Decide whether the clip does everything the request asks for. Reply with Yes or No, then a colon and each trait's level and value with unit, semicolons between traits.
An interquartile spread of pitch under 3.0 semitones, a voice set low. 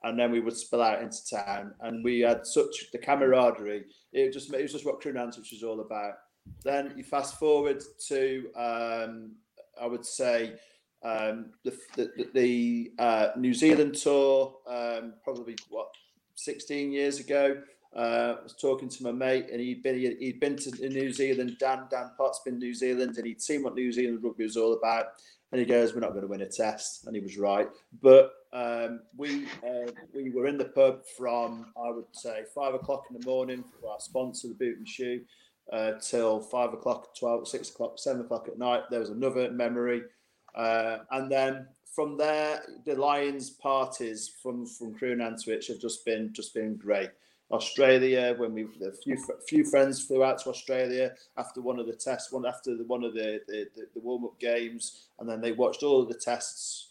Yes: narrow, 2.6 semitones; low, 125 Hz